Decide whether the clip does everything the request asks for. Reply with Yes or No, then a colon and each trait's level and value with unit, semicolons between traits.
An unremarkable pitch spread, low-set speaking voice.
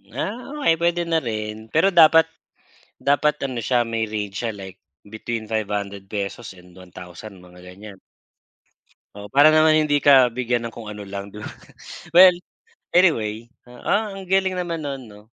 No: wide, 7.3 semitones; low, 115 Hz